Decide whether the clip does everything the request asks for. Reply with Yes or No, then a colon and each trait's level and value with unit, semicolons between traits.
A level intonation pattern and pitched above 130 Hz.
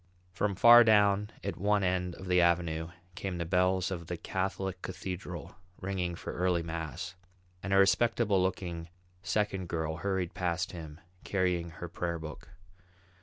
No: narrow, 2.3 semitones; very low, 90 Hz